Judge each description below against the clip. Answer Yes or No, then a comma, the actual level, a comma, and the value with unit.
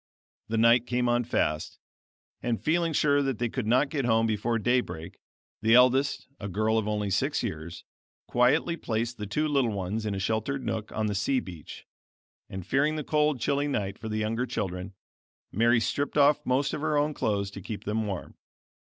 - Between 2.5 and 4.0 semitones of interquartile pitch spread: No, average, 4.7 semitones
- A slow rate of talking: No, average, 195 wpm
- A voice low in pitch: Yes, low, 115 Hz